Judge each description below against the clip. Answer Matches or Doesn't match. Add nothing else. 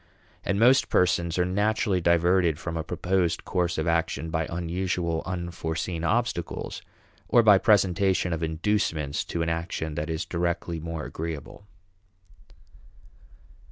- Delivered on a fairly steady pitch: Matches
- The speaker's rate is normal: Doesn't match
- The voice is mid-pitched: Doesn't match